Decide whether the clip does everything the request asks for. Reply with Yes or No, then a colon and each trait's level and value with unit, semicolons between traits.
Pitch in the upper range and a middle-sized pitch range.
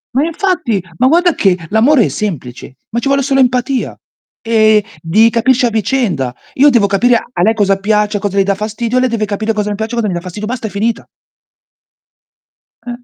Yes: high, 220 Hz; average, 3.6 semitones